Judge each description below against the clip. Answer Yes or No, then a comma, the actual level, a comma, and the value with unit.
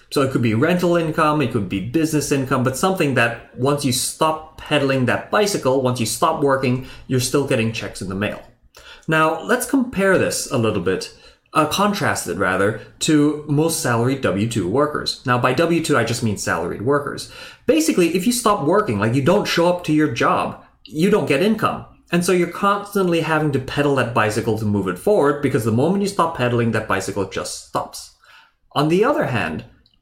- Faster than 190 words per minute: Yes, average, 200 wpm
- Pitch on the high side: No, medium, 140 Hz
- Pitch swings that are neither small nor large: No, wide, 6.1 semitones